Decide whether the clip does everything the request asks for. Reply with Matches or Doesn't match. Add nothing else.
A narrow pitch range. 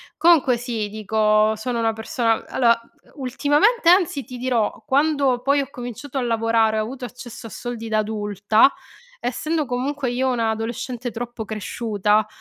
Doesn't match